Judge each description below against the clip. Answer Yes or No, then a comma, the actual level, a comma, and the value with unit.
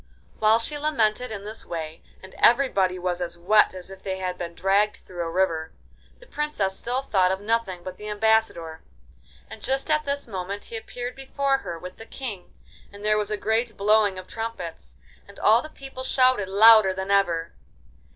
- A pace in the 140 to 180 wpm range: No, average, 190 wpm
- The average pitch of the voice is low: No, high, 205 Hz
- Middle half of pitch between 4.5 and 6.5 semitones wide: No, average, 3.8 semitones